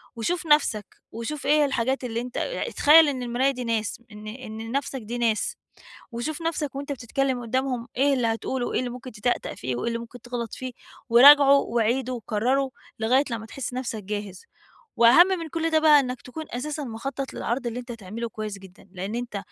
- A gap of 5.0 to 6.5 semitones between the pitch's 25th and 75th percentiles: No, average, 3.3 semitones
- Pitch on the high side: Yes, high, 245 Hz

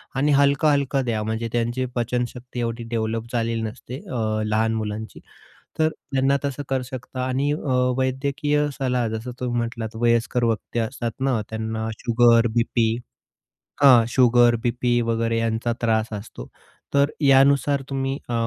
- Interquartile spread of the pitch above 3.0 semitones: No, average, 2.7 semitones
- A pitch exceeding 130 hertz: No, low, 120 Hz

